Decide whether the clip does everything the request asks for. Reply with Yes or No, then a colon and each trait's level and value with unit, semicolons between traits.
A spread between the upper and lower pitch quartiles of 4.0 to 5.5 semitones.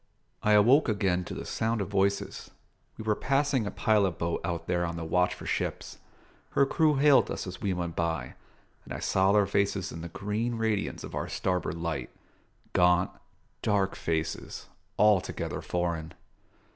No: average, 3.5 semitones